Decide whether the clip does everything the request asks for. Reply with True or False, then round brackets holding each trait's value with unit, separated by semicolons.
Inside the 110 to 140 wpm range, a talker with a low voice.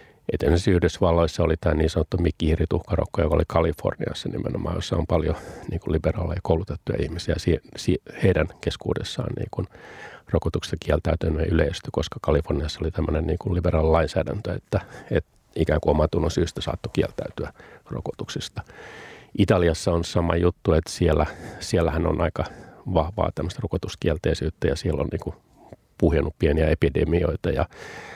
True (115 wpm; 85 Hz)